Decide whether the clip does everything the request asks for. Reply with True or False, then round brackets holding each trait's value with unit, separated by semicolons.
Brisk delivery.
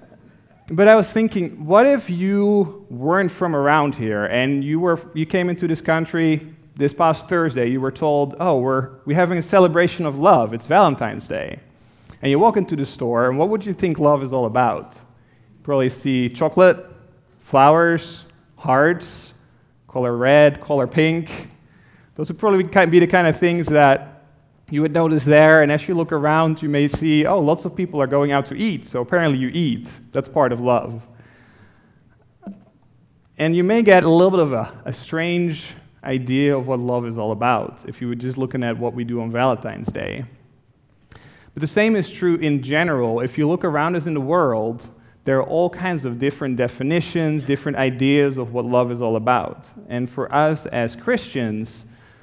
False (185 wpm)